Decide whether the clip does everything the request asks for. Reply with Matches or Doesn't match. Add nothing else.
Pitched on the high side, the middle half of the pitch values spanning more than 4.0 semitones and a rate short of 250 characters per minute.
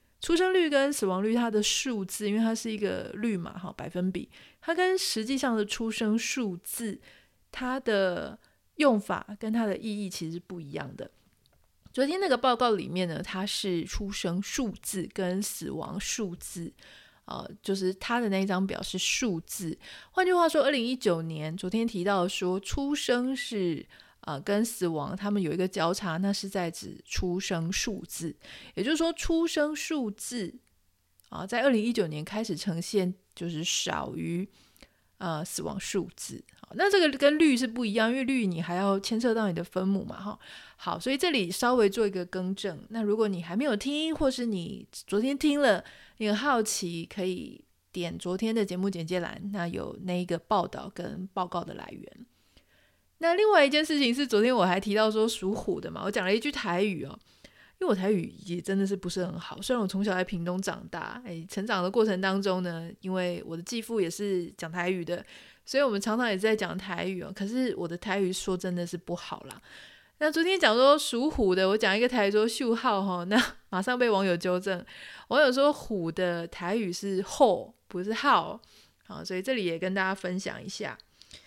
Doesn't match